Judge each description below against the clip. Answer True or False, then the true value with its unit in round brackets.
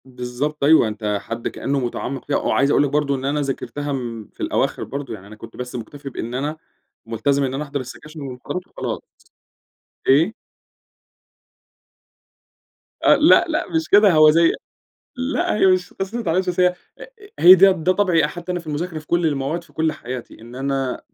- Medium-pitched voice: True (145 Hz)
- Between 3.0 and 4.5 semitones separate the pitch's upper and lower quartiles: False (5.0 semitones)